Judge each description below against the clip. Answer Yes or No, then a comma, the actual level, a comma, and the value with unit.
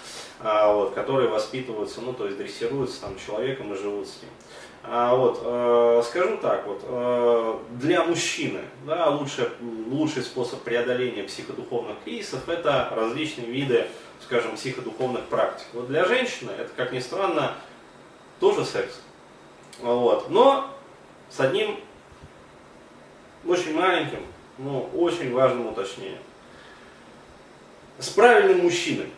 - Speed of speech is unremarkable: Yes, average, 120 wpm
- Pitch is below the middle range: Yes, low, 130 Hz